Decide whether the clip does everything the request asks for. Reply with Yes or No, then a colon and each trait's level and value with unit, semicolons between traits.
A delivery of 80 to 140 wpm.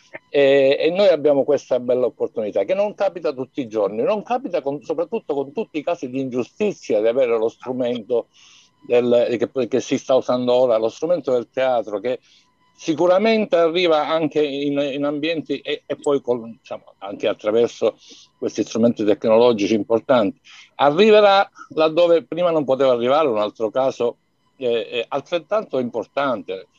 No: average, 150 wpm